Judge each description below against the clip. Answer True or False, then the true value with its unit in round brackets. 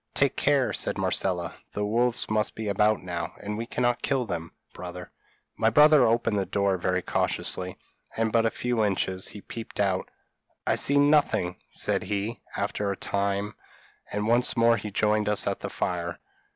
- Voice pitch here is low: True (105 Hz)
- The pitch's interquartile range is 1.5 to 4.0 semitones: True (3.5 semitones)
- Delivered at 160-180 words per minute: True (175 wpm)